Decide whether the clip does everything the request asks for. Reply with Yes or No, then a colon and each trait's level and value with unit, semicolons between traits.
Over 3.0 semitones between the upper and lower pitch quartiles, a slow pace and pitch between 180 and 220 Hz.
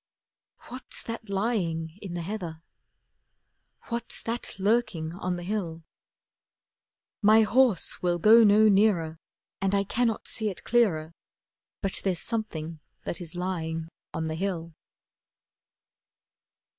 Yes: average, 4.8 semitones; slow, 120 wpm; high, 190 Hz